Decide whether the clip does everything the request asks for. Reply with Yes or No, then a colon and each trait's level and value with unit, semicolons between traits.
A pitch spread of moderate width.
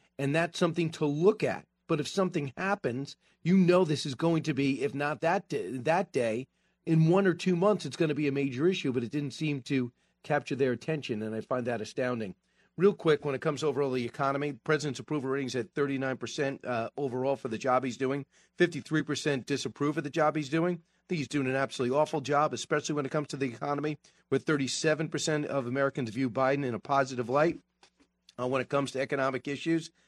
Yes: average, 3.1 semitones